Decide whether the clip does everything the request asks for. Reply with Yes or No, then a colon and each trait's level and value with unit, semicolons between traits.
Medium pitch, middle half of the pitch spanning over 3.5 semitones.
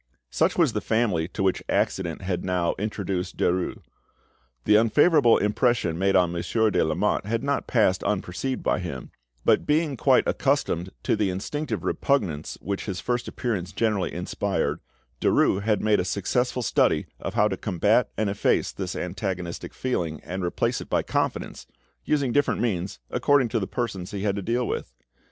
No: low, 100 Hz; average, 4.6 semitones